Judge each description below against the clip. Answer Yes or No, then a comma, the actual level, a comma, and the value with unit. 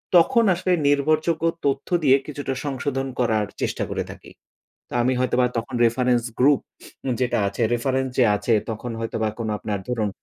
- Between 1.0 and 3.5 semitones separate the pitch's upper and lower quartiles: Yes, average, 3.2 semitones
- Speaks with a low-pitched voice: Yes, low, 130 Hz